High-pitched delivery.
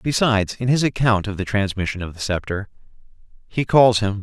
No: low, 110 Hz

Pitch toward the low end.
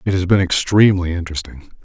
Yes: very low, 90 Hz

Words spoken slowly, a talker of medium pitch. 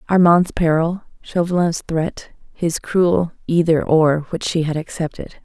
Yes: slow, 120 wpm; medium, 165 Hz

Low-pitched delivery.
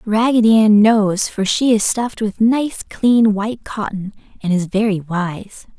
No: high, 210 Hz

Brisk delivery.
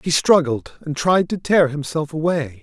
No: average, 185 wpm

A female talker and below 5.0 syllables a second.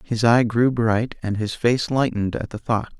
No: male; 4.6 syllables/s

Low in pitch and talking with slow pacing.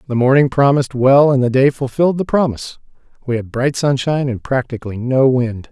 No: low, 130 Hz; average, 190 wpm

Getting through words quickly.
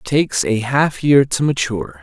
No: average, 180 wpm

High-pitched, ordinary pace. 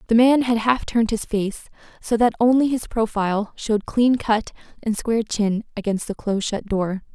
Yes: high, 220 Hz; average, 195 wpm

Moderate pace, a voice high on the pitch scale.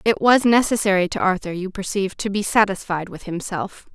Yes: average, 180 wpm; high, 195 Hz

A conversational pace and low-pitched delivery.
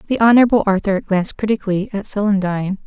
No: average, 145 wpm; high, 200 Hz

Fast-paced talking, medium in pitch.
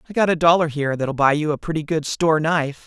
Yes: fast, 275 wpm; medium, 155 Hz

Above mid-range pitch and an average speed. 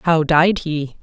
No: medium, 160 Hz; average, 175 wpm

